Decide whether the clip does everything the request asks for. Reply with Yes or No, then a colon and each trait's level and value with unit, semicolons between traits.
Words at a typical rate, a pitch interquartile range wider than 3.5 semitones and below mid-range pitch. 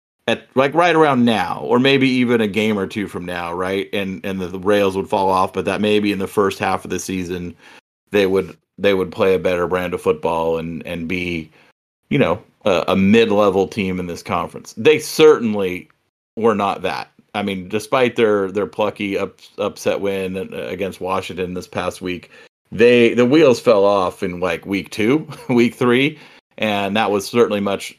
Yes: average, 195 wpm; average, 4.3 semitones; low, 100 Hz